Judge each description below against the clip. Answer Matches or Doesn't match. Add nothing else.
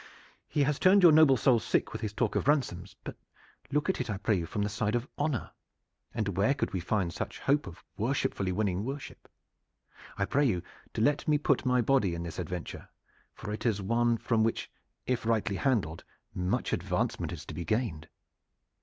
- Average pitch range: Doesn't match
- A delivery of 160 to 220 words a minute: Matches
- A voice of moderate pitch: Doesn't match